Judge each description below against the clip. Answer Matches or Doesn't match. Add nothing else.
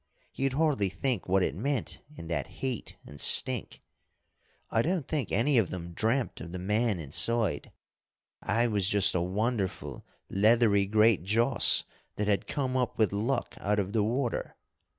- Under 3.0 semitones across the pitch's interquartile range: Doesn't match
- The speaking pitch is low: Matches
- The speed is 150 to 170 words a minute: Matches